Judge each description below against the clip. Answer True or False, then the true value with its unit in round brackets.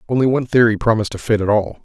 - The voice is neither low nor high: False (115 Hz)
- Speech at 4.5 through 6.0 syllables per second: False (7.9 syllables/s)